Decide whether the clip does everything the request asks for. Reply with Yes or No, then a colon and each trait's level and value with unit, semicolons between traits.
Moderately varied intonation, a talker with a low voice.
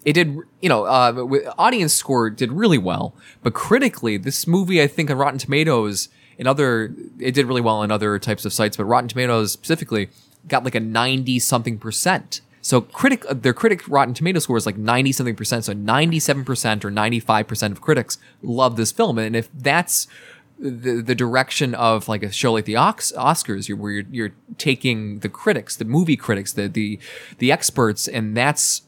Yes: average, 4.3 semitones; low, 125 Hz